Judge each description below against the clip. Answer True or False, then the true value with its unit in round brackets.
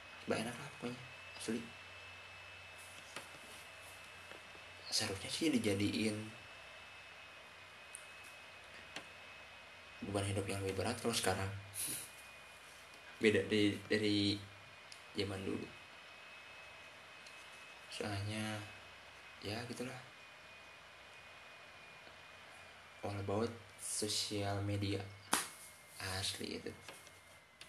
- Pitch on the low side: True (100 Hz)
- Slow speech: True (65 wpm)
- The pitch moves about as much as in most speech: False (1.8 semitones)